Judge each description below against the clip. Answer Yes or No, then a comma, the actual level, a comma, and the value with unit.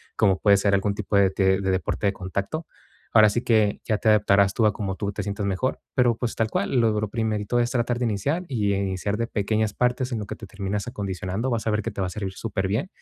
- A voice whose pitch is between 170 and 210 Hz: No, low, 105 Hz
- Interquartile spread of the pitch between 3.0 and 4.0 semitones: No, narrow, 2.6 semitones